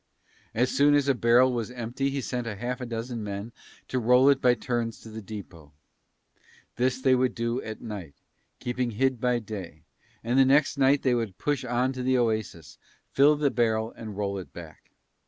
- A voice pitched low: Yes, low, 120 Hz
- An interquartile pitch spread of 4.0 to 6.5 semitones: No, average, 2.9 semitones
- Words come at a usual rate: Yes, average, 190 wpm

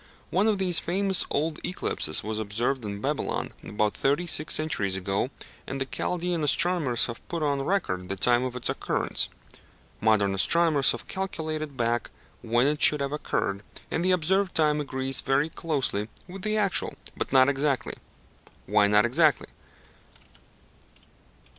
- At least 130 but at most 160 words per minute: Yes, average, 150 wpm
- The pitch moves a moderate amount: No, wide, 6.2 semitones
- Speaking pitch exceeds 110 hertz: Yes, medium, 140 Hz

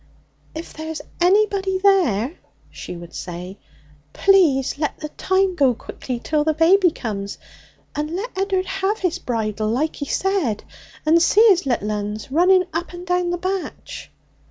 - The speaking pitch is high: Yes, very high, 330 Hz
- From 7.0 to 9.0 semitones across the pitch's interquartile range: Yes, wide, 7.3 semitones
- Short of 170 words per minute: Yes, average, 155 wpm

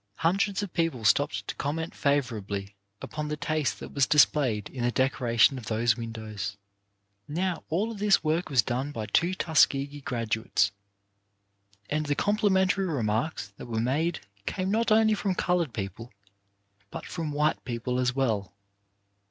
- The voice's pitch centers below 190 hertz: Yes, medium, 140 Hz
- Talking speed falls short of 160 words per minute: Yes, average, 150 wpm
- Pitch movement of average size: No, wide, 6.4 semitones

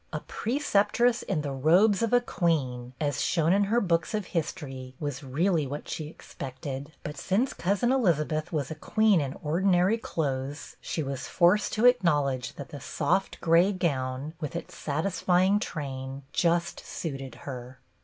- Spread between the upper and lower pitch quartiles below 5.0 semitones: No, wide, 5.6 semitones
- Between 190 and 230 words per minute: No, average, 160 wpm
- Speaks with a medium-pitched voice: Yes, medium, 160 Hz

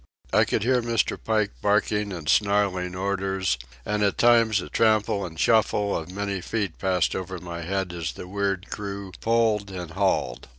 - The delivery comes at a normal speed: Yes, average, 170 wpm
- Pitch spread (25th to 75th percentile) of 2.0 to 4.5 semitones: Yes, narrow, 2.5 semitones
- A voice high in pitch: No, low, 100 Hz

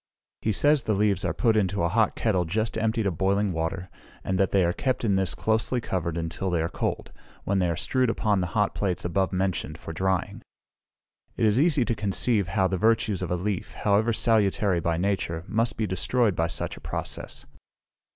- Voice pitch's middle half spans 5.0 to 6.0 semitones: No, average, 3.8 semitones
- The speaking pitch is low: Yes, low, 100 Hz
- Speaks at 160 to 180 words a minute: No, fast, 205 wpm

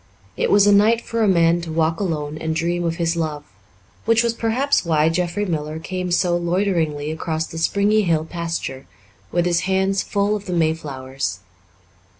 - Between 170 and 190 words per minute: Yes, average, 175 wpm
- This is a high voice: No, medium, 170 Hz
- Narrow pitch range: No, average, 3.7 semitones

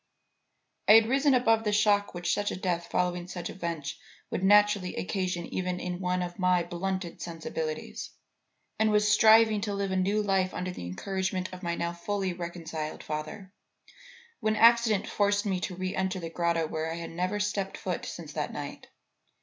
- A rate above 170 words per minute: Yes, average, 180 wpm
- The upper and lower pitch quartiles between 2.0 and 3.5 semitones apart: Yes, average, 2.9 semitones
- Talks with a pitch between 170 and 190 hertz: Yes, medium, 185 Hz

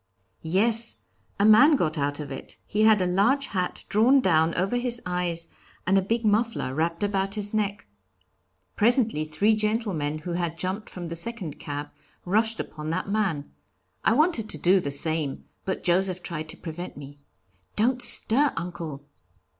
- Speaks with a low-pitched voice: No, medium, 185 Hz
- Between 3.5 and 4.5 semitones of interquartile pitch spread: No, average, 5.1 semitones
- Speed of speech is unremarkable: Yes, average, 165 wpm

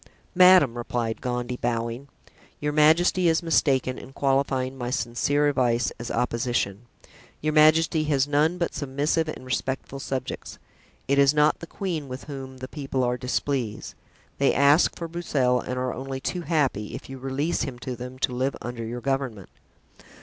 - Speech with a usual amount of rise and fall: Yes, average, 3.1 semitones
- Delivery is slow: No, average, 165 wpm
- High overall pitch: No, low, 135 Hz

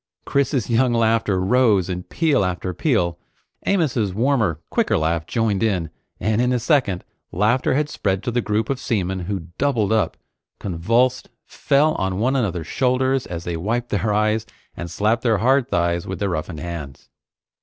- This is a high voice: No, low, 110 Hz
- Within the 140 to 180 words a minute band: Yes, average, 165 wpm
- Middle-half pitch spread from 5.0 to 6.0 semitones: Yes, wide, 5.5 semitones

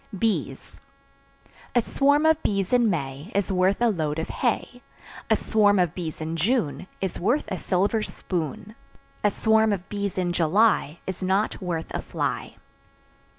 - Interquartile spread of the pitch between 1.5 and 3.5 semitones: No, average, 4.2 semitones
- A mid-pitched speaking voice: No, high, 195 Hz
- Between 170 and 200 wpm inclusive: No, average, 155 wpm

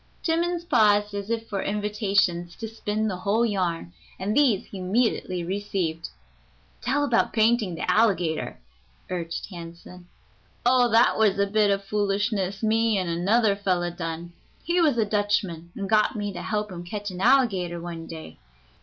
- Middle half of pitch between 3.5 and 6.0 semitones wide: Yes, average, 3.8 semitones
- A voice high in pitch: Yes, high, 200 Hz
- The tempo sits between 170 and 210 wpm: No, average, 160 wpm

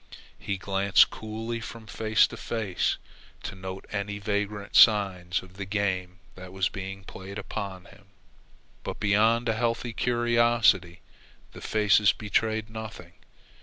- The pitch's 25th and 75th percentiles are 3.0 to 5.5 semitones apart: No, narrow, 2.6 semitones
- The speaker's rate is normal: No, slow, 130 wpm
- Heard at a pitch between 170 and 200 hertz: No, low, 100 Hz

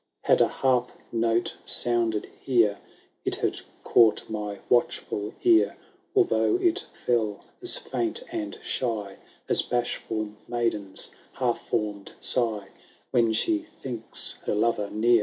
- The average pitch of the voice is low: Yes, low, 115 Hz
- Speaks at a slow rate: Yes, slow, 120 wpm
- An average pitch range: Yes, average, 3.2 semitones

